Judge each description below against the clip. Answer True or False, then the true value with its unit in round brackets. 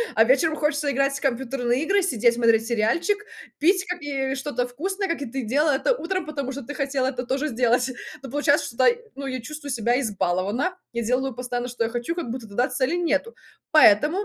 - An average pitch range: True (3.8 semitones)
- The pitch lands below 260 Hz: False (270 Hz)